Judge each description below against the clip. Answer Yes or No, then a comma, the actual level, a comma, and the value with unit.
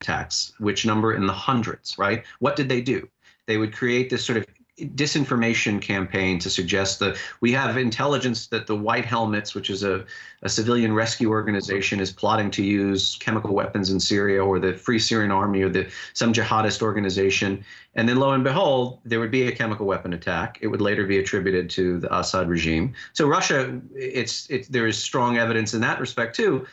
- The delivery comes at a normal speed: Yes, average, 195 wpm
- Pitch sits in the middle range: No, low, 110 Hz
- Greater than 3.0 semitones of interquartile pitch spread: Yes, average, 3.5 semitones